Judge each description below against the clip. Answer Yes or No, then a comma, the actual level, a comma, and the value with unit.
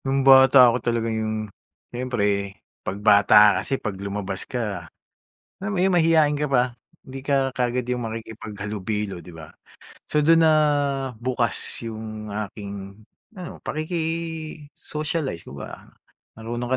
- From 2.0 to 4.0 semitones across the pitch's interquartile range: No, wide, 5.5 semitones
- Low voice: Yes, low, 120 Hz